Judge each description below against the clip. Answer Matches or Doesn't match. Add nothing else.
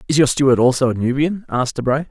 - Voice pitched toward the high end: Doesn't match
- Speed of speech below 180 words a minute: Doesn't match